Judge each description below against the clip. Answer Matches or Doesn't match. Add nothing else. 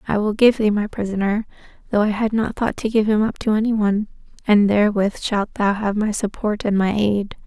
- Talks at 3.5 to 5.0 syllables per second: Doesn't match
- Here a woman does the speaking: Matches